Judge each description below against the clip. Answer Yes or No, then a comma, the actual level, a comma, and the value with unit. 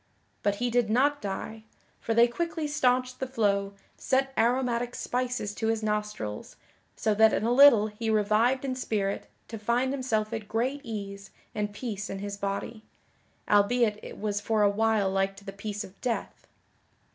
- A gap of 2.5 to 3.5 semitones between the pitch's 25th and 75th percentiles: Yes, average, 3.2 semitones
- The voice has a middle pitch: No, high, 220 Hz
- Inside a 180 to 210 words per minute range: No, average, 170 wpm